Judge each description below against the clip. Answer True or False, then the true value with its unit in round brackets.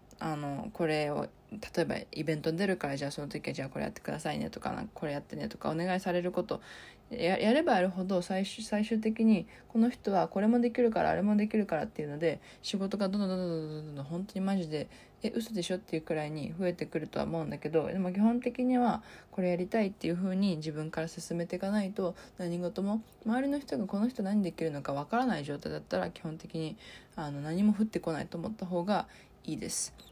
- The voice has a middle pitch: True (180 Hz)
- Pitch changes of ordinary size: True (4.7 semitones)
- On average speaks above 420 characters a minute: True (455 characters per minute)